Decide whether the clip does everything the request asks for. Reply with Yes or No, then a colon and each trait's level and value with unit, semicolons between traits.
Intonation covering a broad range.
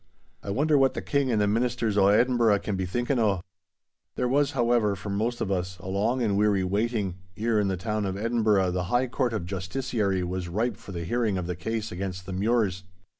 No: average, 4.0 semitones